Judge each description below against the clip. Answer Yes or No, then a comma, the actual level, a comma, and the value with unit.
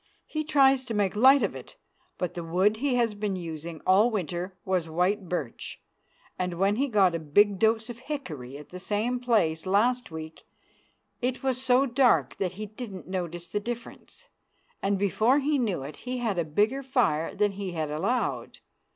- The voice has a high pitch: Yes, high, 205 Hz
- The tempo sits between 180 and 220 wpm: Yes, average, 185 wpm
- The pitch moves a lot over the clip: Yes, wide, 6.0 semitones